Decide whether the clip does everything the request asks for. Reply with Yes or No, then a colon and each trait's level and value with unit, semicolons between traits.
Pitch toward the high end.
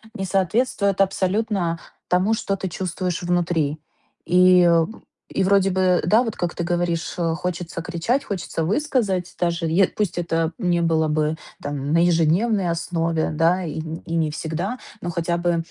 No: medium, 175 Hz